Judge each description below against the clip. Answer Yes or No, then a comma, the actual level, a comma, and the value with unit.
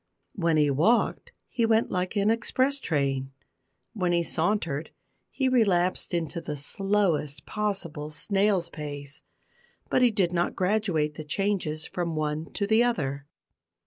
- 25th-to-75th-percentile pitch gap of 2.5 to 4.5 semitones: No, wide, 5.5 semitones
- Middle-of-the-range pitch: Yes, medium, 175 Hz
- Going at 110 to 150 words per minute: Yes, average, 140 wpm